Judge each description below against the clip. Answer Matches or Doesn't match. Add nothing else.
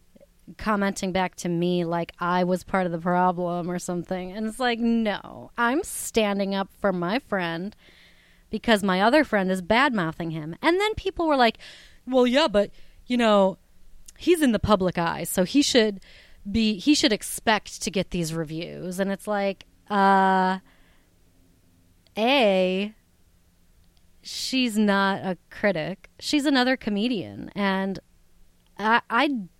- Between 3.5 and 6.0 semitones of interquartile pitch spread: Matches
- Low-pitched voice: Doesn't match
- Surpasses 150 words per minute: Doesn't match